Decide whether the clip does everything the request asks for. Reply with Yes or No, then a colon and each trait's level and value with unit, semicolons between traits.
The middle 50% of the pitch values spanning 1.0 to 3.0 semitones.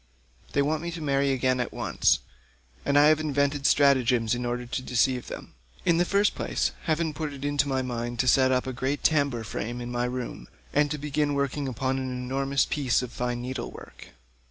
Yes: average, 2.7 semitones